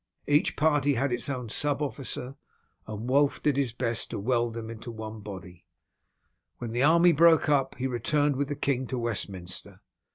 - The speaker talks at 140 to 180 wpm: Yes, average, 175 wpm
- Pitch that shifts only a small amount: No, average, 4.0 semitones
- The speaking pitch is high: No, low, 130 Hz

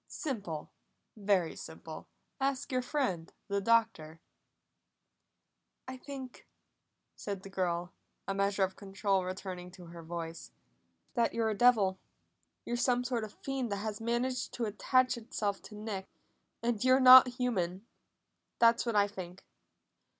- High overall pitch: Yes, high, 210 Hz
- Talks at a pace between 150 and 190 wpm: No, average, 140 wpm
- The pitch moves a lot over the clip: No, average, 4.6 semitones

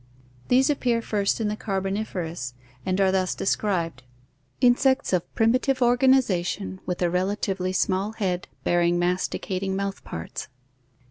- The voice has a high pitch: Yes, high, 195 Hz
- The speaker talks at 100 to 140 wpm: Yes, slow, 135 wpm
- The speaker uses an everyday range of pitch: Yes, average, 3.7 semitones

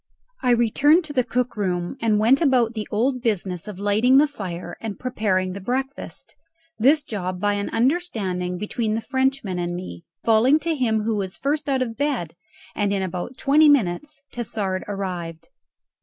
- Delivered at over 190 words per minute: No, average, 170 wpm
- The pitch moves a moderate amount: No, wide, 5.8 semitones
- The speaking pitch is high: Yes, high, 220 Hz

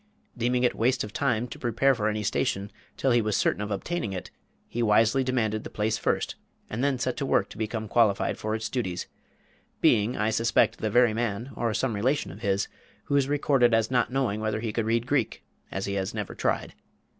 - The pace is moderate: No, fast, 215 wpm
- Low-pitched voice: Yes, low, 115 Hz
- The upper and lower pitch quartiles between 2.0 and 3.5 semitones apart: Yes, average, 2.8 semitones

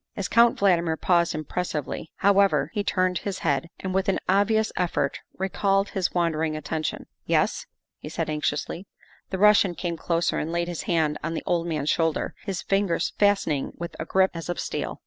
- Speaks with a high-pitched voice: No, medium, 175 Hz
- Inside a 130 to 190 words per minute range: No, average, 200 wpm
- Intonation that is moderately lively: Yes, average, 3.3 semitones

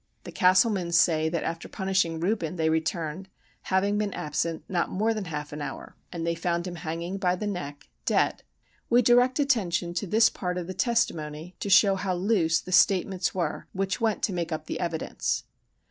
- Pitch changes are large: No, average, 3.2 semitones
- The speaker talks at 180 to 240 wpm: Yes, average, 190 wpm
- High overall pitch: No, medium, 180 Hz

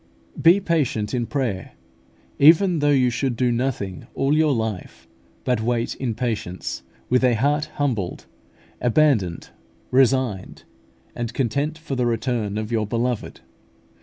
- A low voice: Yes, low, 125 Hz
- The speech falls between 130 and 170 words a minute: Yes, slow, 135 wpm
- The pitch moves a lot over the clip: No, average, 4.0 semitones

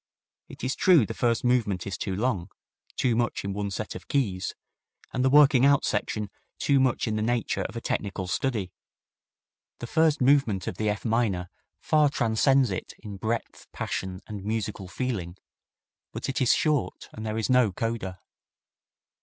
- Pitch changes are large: No, average, 4.6 semitones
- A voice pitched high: No, low, 115 Hz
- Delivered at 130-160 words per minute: No, average, 170 wpm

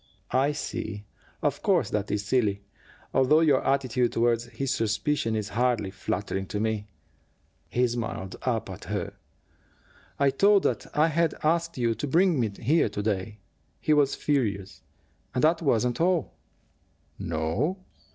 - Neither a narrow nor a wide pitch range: No, wide, 5.8 semitones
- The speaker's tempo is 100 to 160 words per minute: Yes, average, 150 wpm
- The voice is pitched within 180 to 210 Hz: No, low, 120 Hz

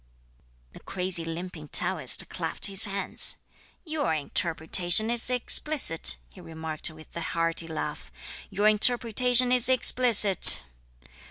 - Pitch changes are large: Yes, wide, 6.5 semitones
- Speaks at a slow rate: Yes, slow, 110 wpm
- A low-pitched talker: No, high, 190 Hz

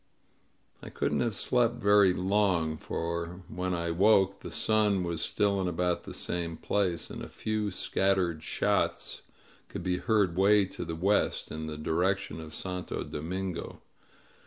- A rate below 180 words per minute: Yes, average, 160 wpm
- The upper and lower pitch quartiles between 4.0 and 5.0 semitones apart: No, average, 3.1 semitones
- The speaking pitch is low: Yes, very low, 90 Hz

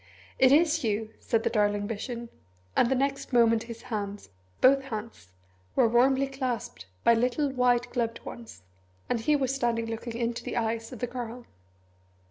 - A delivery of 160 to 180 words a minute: Yes, average, 165 wpm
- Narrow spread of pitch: Yes, narrow, 2.2 semitones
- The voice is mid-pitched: No, high, 235 Hz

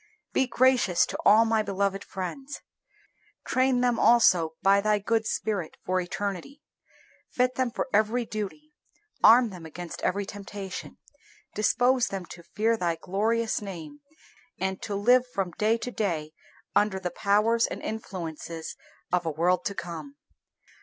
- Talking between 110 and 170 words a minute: Yes, average, 145 wpm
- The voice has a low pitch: No, high, 205 Hz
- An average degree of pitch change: Yes, average, 4.2 semitones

